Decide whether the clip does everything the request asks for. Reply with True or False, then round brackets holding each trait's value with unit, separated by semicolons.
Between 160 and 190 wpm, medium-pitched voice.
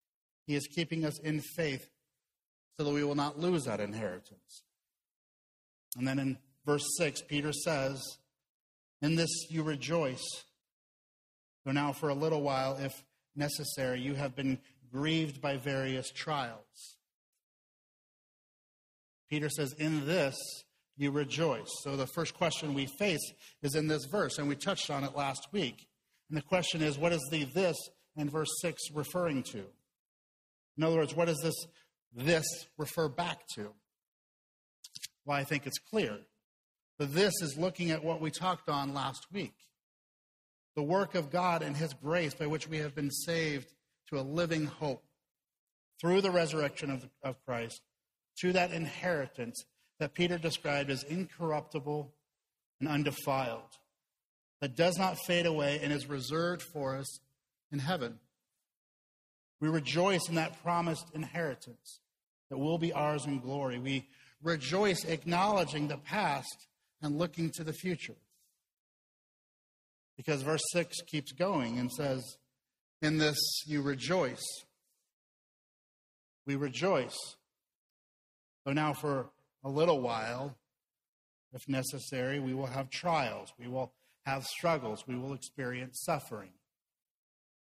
False (140 wpm; 150 Hz)